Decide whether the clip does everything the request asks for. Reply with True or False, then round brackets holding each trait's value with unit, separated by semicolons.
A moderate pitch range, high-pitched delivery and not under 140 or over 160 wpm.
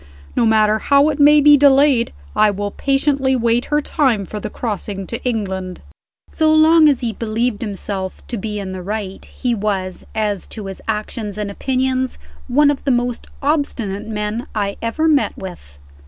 False (4.9 semitones; 230 Hz; 175 wpm)